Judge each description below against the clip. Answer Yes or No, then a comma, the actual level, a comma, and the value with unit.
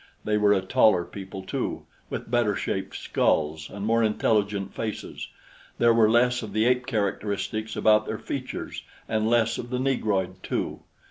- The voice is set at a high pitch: No, low, 110 Hz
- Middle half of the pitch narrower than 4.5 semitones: Yes, narrow, 2.6 semitones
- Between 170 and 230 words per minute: No, average, 160 wpm